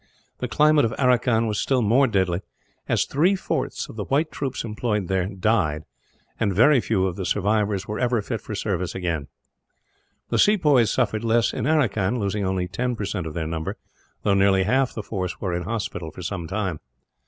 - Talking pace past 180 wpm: Yes, average, 190 wpm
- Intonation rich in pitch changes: No, average, 4.6 semitones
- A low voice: Yes, low, 105 Hz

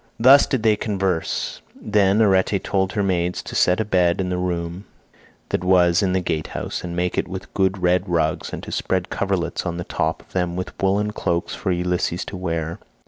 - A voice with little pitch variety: Yes, narrow, 2.0 semitones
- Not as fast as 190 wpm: No, average, 200 wpm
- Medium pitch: No, very low, 90 Hz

